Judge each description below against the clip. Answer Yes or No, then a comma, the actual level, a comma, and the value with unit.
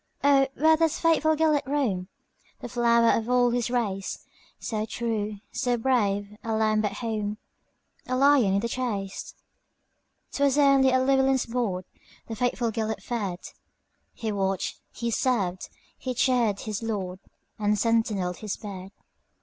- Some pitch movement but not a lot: Yes, average, 3.7 semitones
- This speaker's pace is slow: Yes, slow, 120 wpm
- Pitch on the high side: Yes, high, 230 Hz